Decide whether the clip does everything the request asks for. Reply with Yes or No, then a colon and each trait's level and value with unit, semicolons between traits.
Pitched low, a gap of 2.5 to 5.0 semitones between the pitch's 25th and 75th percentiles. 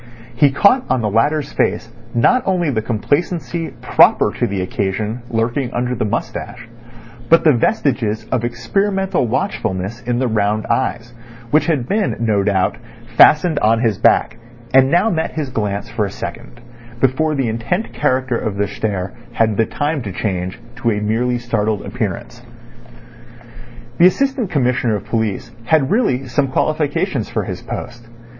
No: low, 120 Hz; wide, 5.4 semitones